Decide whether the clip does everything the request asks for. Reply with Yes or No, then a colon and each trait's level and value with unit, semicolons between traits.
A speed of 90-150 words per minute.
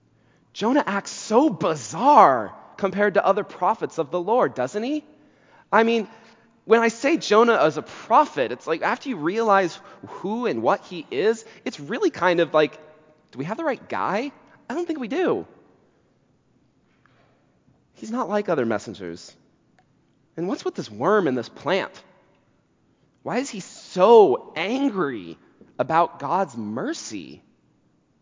Yes: average, 145 wpm